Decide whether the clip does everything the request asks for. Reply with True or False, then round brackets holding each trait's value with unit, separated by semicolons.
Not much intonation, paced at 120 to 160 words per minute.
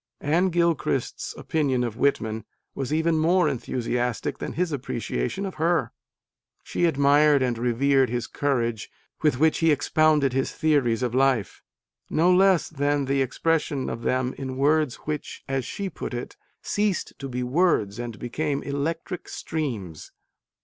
False (4.3 semitones; 150 wpm)